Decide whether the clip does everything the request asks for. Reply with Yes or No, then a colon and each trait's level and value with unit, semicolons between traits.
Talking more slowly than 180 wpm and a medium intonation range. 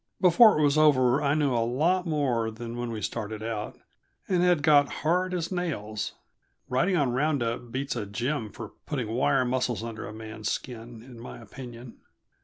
No: average, 185 wpm; average, 4.8 semitones